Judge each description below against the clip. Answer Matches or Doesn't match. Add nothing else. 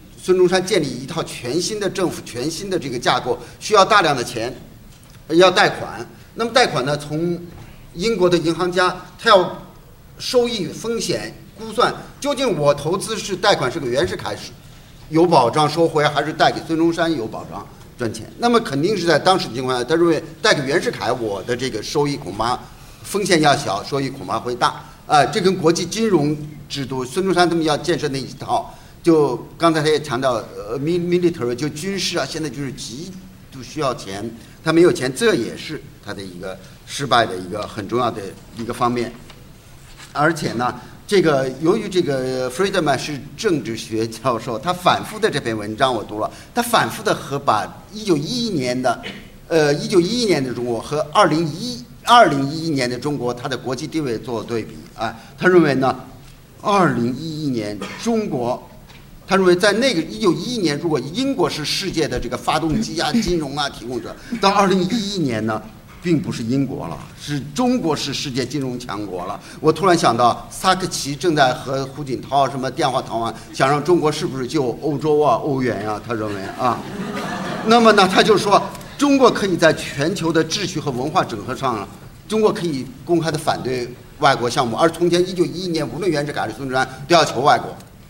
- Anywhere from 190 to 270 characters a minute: Doesn't match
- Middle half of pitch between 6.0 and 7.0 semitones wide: Doesn't match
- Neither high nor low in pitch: Matches